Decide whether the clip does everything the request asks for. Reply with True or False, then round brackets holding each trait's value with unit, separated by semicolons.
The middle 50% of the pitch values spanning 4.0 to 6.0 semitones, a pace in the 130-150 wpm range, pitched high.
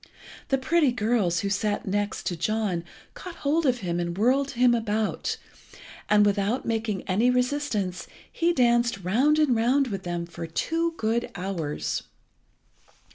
True (5.1 semitones; 140 wpm; 220 Hz)